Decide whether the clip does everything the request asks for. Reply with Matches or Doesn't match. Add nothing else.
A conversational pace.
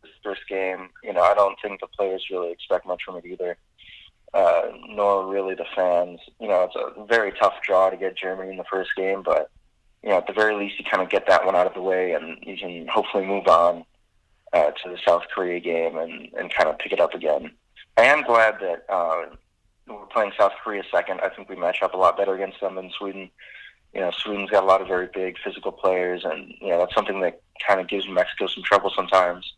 Doesn't match